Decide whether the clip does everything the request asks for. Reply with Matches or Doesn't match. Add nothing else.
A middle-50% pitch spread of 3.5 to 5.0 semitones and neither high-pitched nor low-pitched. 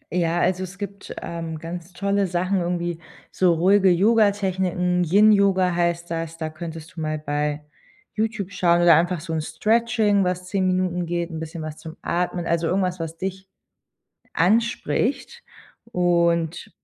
Doesn't match